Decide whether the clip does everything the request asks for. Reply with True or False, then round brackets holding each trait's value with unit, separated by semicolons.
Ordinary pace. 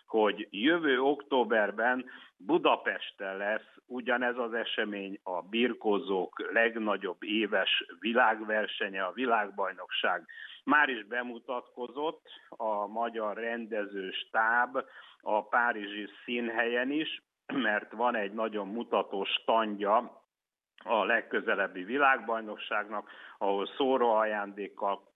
False (90 wpm)